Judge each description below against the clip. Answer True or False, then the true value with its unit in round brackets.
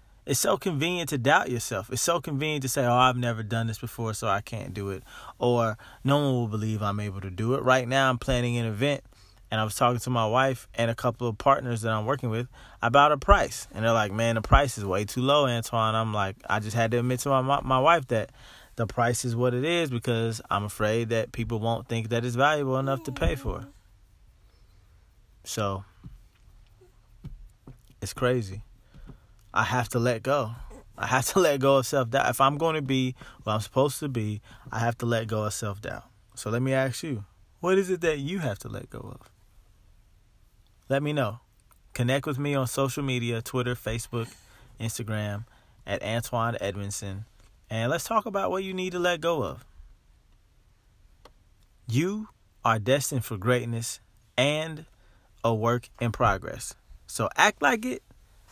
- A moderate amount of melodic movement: True (3.9 semitones)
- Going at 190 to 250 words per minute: True (195 wpm)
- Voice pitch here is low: True (115 Hz)